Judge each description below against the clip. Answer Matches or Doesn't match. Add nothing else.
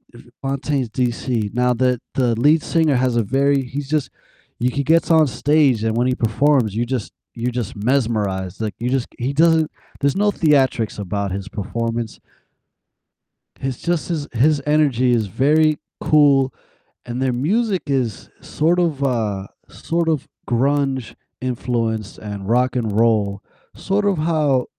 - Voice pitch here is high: Doesn't match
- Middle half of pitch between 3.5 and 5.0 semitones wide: Matches